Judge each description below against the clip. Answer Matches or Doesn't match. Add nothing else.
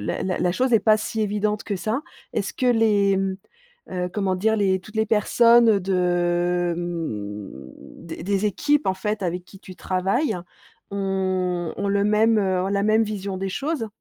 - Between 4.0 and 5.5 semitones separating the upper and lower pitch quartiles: Doesn't match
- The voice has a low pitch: Doesn't match